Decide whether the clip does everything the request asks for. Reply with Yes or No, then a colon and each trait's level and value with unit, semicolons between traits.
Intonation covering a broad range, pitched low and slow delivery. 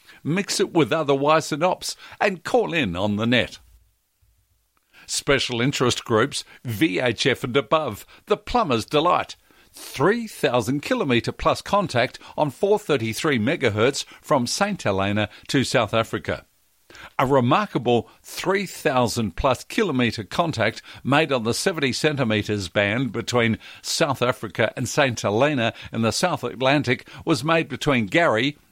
Yes: wide, 5.8 semitones; low, 125 Hz; slow, 125 wpm